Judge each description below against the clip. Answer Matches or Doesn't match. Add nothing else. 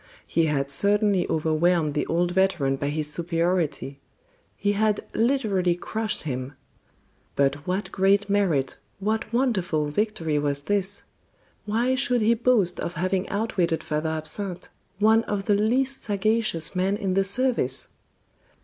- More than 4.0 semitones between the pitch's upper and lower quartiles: Matches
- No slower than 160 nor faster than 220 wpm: Doesn't match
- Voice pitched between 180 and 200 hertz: Matches